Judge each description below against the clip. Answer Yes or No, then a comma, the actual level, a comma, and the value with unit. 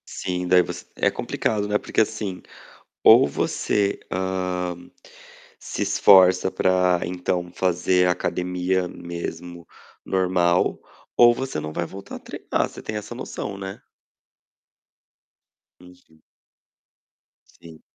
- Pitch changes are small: Yes, narrow, 1.4 semitones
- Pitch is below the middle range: Yes, very low, 90 Hz